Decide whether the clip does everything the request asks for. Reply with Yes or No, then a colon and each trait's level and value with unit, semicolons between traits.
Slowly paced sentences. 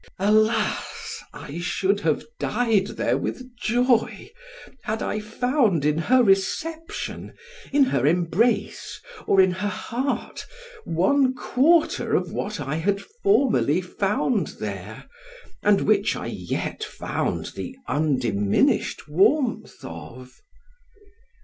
Yes: slow, 110 wpm